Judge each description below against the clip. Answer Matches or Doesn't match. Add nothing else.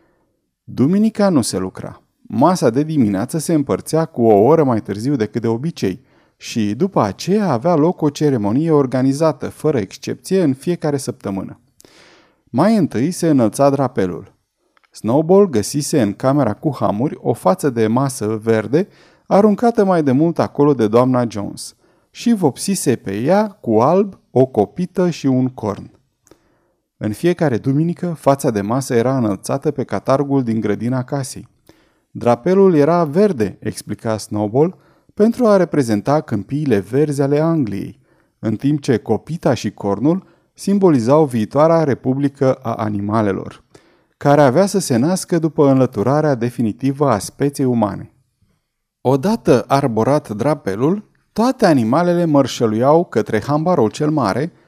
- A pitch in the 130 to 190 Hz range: Matches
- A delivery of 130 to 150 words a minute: Matches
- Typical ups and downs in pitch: Doesn't match